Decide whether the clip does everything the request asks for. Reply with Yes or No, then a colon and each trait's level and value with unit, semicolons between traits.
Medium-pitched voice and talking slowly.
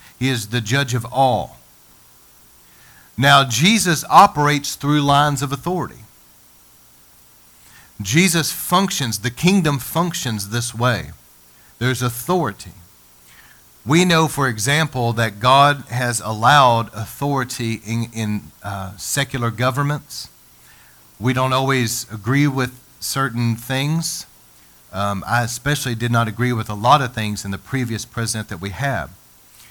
No: low, 120 Hz; slow, 125 wpm